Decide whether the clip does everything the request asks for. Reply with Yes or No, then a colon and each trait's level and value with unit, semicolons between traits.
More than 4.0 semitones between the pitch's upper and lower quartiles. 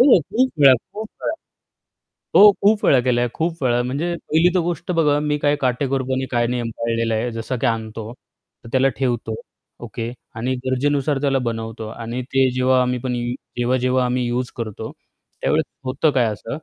No: average, 3.3 semitones